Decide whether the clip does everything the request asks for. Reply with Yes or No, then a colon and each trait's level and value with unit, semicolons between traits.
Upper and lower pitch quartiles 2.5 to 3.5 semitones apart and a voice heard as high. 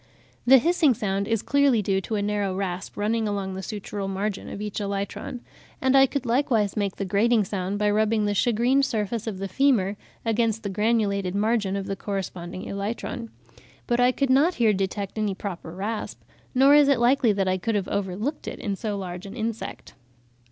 Yes: average, 3.2 semitones; high, 210 Hz